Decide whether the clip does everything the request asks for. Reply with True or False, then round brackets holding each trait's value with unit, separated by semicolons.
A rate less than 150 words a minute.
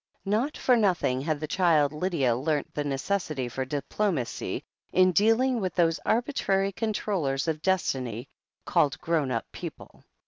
True (140 wpm)